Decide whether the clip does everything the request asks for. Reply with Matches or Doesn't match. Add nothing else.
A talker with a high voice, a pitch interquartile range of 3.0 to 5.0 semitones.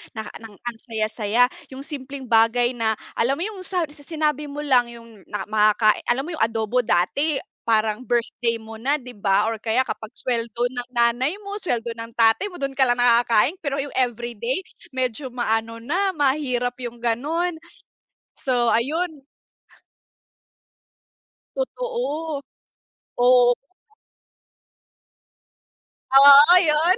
Matches